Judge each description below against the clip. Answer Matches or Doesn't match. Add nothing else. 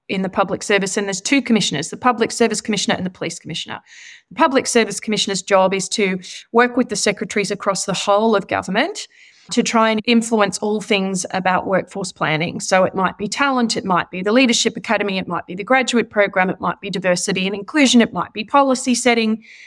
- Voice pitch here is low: Doesn't match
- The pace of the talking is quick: Matches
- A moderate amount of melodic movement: Matches